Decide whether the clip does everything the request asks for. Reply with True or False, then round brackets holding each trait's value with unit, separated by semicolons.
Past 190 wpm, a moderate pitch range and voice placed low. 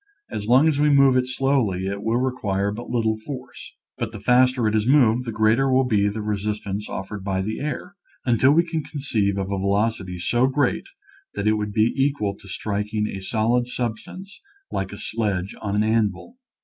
True (200 wpm; 4.0 semitones; 110 Hz)